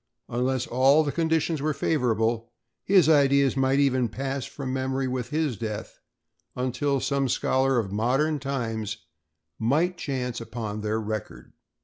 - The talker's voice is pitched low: Yes, low, 130 Hz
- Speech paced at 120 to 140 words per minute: Yes, slow, 135 wpm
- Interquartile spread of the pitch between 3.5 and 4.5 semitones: No, average, 3.1 semitones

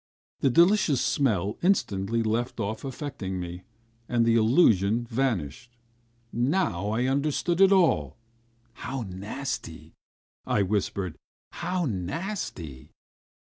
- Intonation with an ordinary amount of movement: No, wide, 6.4 semitones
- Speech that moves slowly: Yes, slow, 100 wpm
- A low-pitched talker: Yes, low, 115 Hz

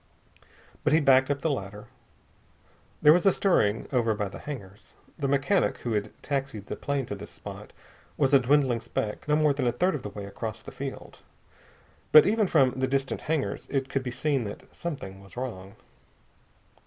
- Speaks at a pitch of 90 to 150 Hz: Yes, low, 135 Hz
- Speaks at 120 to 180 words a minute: No, average, 190 wpm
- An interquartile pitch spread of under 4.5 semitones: No, average, 5.1 semitones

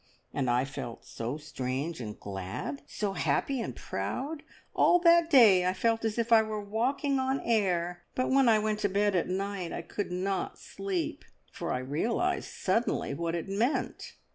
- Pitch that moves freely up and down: Yes, wide, 6.0 semitones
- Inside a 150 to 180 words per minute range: Yes, average, 175 wpm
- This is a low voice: No, high, 195 Hz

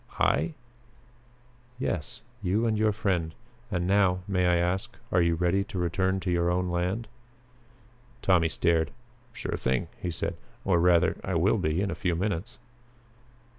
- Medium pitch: No, very low, 90 Hz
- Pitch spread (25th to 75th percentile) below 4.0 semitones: Yes, narrow, 2.4 semitones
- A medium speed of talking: Yes, average, 155 wpm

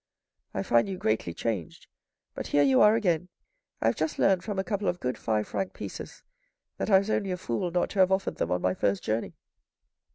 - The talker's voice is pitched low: No, medium, 165 Hz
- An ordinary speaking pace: No, fast, 225 wpm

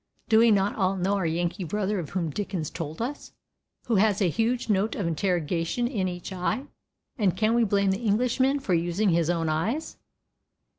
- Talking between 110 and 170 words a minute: No, average, 190 wpm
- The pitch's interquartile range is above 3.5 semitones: Yes, average, 4.2 semitones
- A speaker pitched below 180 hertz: No, high, 195 Hz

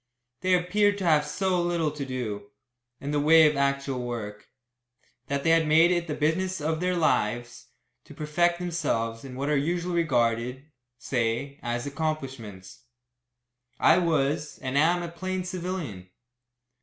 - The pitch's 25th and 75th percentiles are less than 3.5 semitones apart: No, wide, 5.4 semitones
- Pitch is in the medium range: Yes, medium, 150 Hz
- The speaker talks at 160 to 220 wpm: No, average, 150 wpm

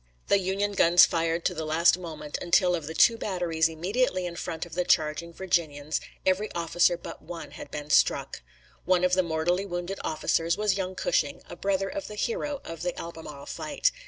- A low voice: No, medium, 175 Hz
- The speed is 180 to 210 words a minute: Yes, average, 190 wpm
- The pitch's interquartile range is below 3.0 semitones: Yes, narrow, 2.6 semitones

